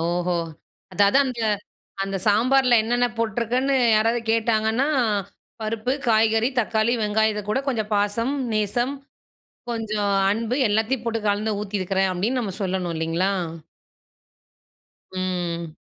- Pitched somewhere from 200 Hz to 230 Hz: Yes, high, 215 Hz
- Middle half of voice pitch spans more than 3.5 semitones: No, average, 2.8 semitones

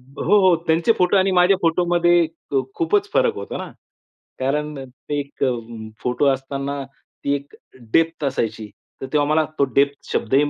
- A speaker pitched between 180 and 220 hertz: No, medium, 150 Hz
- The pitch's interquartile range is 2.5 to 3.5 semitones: No, average, 4.2 semitones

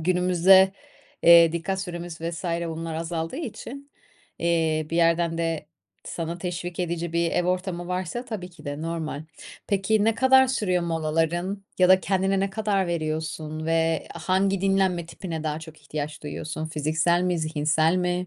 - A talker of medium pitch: Yes, medium, 170 Hz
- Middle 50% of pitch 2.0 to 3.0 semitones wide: Yes, narrow, 2.5 semitones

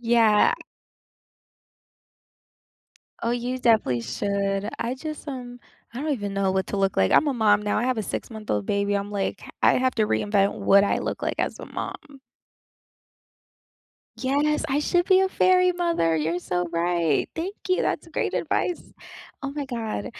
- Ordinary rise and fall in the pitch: No, wide, 5.8 semitones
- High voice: Yes, high, 225 Hz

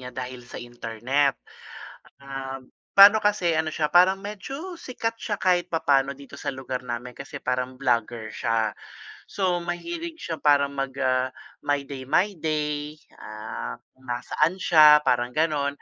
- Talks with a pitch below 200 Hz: Yes, medium, 140 Hz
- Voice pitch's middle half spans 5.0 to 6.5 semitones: Yes, wide, 5.5 semitones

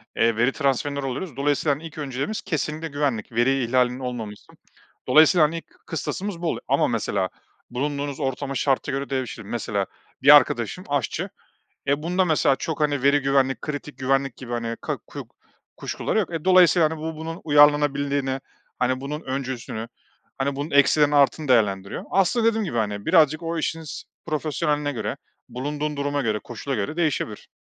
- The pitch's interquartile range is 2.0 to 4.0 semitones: Yes, average, 3.3 semitones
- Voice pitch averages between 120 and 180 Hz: Yes, medium, 140 Hz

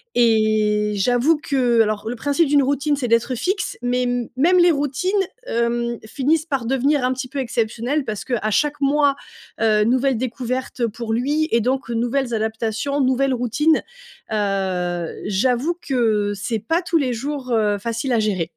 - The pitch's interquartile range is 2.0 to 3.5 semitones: No, average, 4.0 semitones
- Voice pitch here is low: No, high, 245 Hz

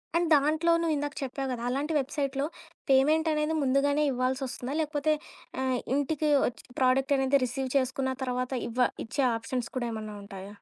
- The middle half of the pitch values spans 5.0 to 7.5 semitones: No, narrow, 2.4 semitones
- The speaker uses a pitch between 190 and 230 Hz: No, very high, 270 Hz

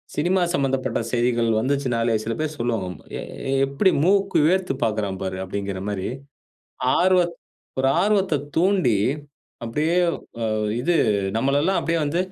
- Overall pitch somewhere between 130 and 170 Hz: Yes, low, 135 Hz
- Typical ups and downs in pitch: No, wide, 7.3 semitones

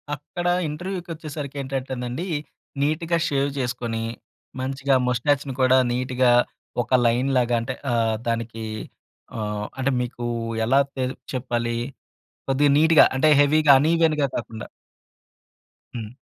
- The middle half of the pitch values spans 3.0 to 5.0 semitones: Yes, average, 3.5 semitones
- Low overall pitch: Yes, low, 130 Hz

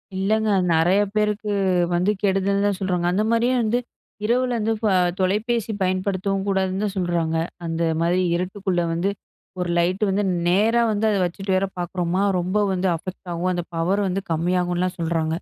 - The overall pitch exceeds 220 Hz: No, high, 190 Hz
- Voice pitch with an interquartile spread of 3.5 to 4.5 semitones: No, average, 2.8 semitones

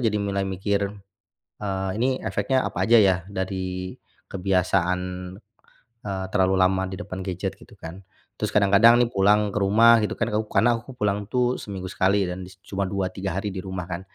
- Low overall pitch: Yes, low, 100 Hz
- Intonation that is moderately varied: No, narrow, 1.8 semitones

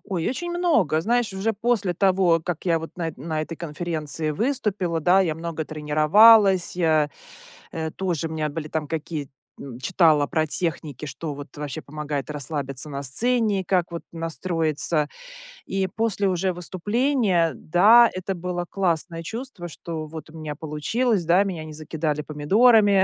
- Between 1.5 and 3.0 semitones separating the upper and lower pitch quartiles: No, average, 4.0 semitones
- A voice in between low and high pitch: Yes, medium, 170 Hz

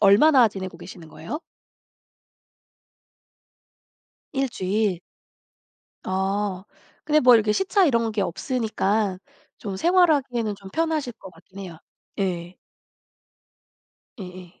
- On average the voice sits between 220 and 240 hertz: No, high, 205 Hz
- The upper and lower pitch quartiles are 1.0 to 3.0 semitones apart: No, average, 5.2 semitones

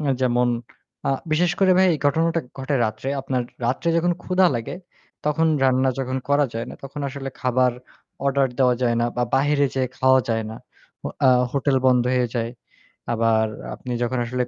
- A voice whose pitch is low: Yes, low, 130 Hz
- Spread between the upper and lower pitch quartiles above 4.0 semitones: No, average, 2.7 semitones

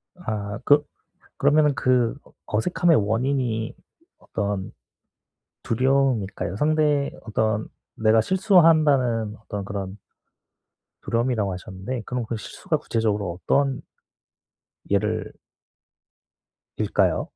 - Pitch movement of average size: Yes, average, 5.0 semitones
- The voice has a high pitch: No, low, 115 Hz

